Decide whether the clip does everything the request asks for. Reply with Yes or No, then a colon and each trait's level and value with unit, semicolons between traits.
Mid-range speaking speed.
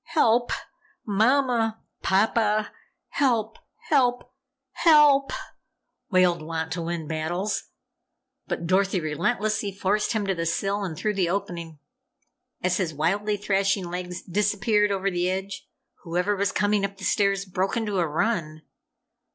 No: slow, 125 wpm